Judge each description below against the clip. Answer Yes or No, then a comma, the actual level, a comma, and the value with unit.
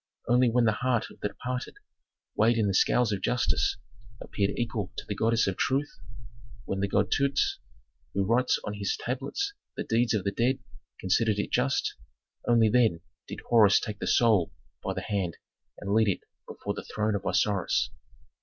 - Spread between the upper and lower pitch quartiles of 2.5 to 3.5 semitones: Yes, average, 3.1 semitones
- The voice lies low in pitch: Yes, low, 110 Hz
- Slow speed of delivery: No, average, 180 wpm